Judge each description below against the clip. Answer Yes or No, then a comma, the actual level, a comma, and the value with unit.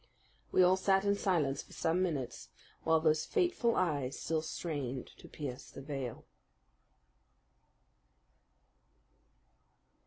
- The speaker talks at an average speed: No, slow, 105 wpm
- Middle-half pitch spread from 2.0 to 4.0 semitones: No, average, 5.2 semitones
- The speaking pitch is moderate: Yes, medium, 160 Hz